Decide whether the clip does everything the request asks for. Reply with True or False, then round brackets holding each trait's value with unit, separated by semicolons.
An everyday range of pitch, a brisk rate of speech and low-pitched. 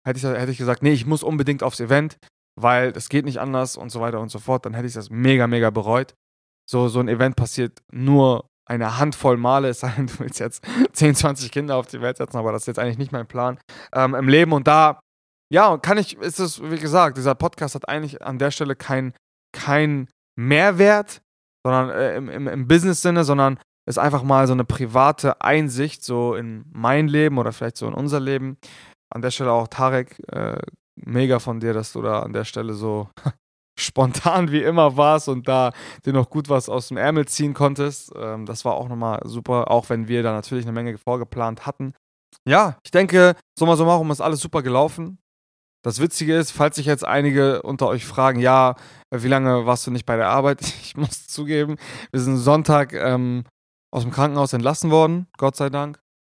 True (3.3 semitones; 205 wpm; 130 Hz)